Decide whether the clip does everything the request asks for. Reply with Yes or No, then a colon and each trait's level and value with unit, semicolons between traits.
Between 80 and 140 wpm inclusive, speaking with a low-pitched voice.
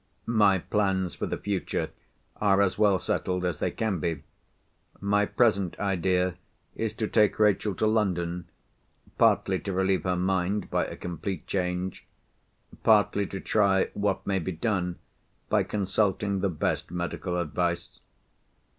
Yes: slow, 135 wpm; very low, 95 Hz